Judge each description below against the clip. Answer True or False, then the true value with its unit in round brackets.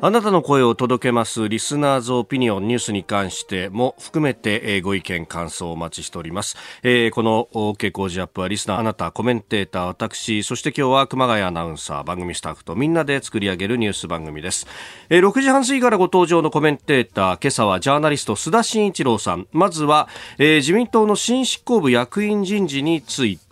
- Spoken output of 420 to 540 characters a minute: True (430 characters per minute)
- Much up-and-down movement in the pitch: True (7.6 semitones)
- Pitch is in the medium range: False (120 Hz)